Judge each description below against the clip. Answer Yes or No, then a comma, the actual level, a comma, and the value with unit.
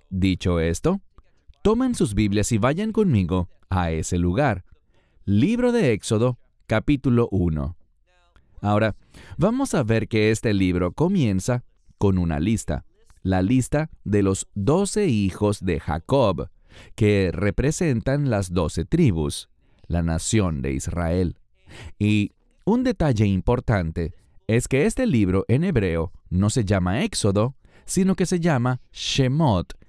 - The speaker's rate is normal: No, slow, 125 wpm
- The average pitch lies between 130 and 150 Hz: No, low, 105 Hz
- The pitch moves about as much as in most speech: No, wide, 6.6 semitones